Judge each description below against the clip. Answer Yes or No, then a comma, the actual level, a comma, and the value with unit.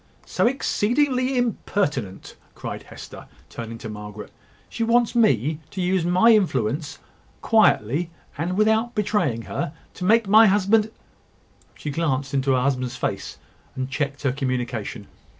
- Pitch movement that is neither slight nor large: No, wide, 8.9 semitones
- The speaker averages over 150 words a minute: No, slow, 135 wpm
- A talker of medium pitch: Yes, medium, 160 Hz